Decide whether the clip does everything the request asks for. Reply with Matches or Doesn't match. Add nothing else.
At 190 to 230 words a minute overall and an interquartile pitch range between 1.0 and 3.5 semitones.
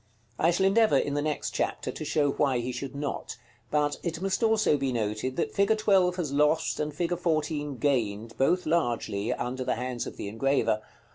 Doesn't match